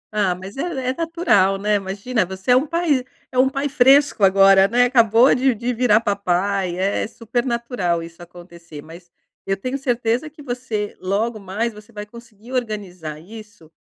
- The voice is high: Yes, high, 215 Hz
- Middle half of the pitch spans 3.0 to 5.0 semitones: Yes, average, 4.5 semitones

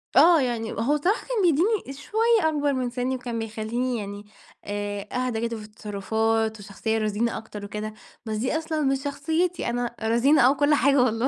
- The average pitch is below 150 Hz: No, high, 245 Hz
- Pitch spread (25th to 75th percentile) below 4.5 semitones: No, average, 4.8 semitones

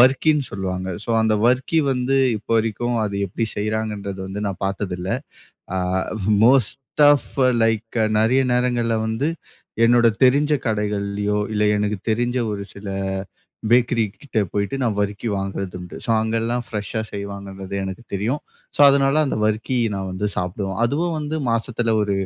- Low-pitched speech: Yes, low, 110 Hz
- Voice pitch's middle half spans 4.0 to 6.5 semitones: No, average, 3.6 semitones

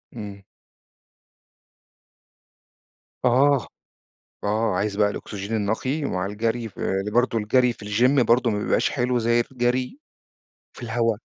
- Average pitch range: Yes, average, 3.2 semitones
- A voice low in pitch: Yes, low, 115 Hz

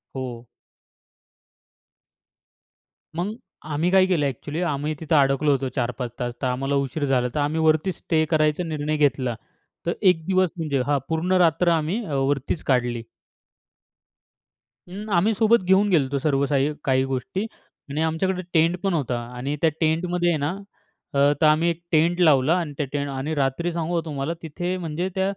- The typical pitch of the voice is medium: Yes, medium, 155 Hz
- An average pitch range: Yes, average, 3.9 semitones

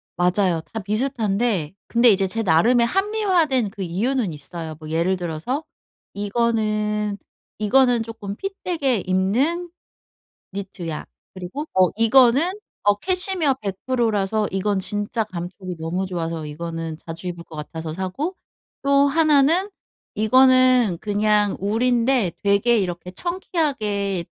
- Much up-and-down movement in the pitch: Yes, wide, 5.8 semitones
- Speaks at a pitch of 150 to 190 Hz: No, high, 210 Hz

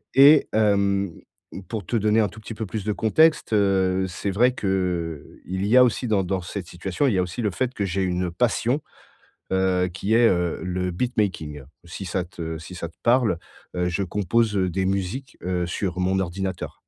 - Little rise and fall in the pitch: No, average, 3.4 semitones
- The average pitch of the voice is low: Yes, very low, 95 Hz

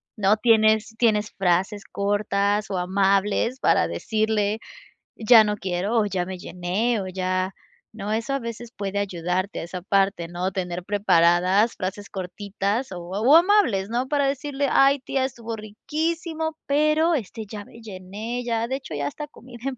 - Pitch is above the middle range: Yes, high, 210 Hz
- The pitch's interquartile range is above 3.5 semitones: Yes, average, 4.0 semitones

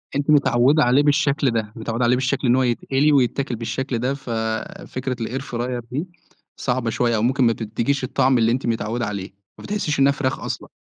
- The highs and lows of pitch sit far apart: No, average, 2.7 semitones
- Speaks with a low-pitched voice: Yes, low, 125 Hz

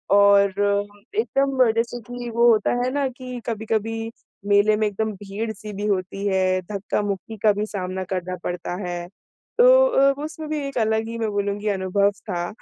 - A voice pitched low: No, high, 210 Hz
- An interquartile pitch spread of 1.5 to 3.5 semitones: Yes, average, 2.9 semitones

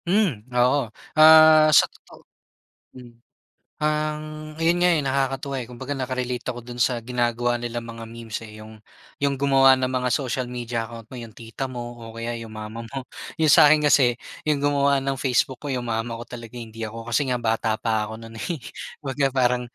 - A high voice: No, low, 125 Hz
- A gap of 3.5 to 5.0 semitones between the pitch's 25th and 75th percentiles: No, average, 3.0 semitones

